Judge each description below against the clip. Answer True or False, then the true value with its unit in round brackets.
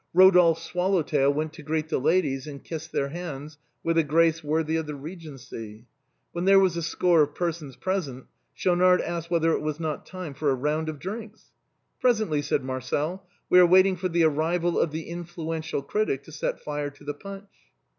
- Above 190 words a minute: True (200 wpm)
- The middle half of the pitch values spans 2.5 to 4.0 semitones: True (3.3 semitones)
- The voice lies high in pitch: False (160 Hz)